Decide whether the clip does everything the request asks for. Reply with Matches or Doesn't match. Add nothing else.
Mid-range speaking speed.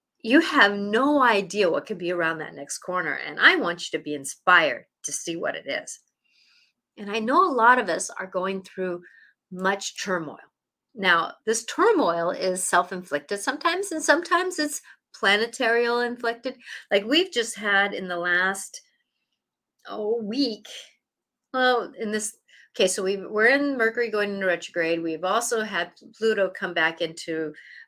Matches